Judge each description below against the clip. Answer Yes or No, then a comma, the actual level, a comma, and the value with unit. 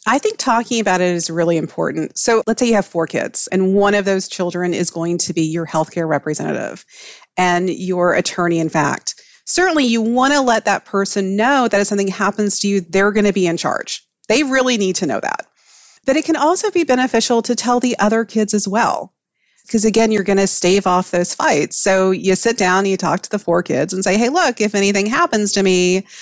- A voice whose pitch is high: Yes, high, 200 Hz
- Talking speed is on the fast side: Yes, fast, 225 wpm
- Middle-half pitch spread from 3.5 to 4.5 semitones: Yes, average, 4.2 semitones